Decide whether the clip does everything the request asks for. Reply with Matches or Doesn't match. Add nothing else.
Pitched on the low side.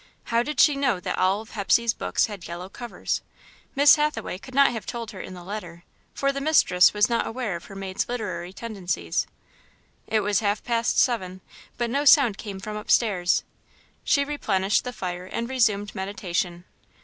Doesn't match